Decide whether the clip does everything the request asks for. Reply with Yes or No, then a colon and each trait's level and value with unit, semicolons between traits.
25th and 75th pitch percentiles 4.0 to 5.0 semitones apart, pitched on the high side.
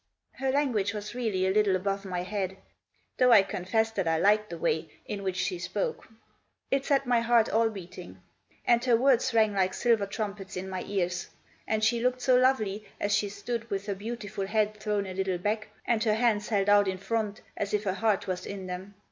No: average, 2.9 semitones; high, 205 Hz